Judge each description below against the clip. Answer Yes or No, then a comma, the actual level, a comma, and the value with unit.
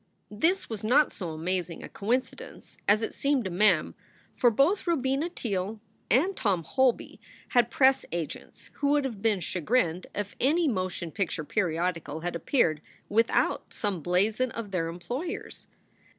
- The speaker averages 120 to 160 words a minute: Yes, average, 150 wpm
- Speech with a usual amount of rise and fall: No, wide, 6.7 semitones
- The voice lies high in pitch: Yes, high, 210 Hz